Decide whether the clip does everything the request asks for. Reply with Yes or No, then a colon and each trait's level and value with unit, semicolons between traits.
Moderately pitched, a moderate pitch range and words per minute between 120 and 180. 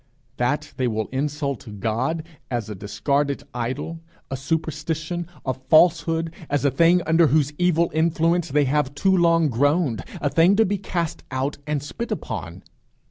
Yes: medium, 150 Hz; average, 3.9 semitones; average, 155 wpm